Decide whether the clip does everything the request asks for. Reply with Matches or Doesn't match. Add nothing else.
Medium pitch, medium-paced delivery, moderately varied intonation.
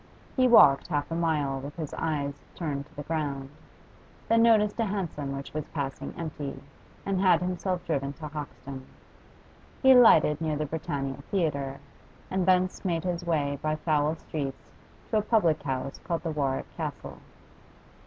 Matches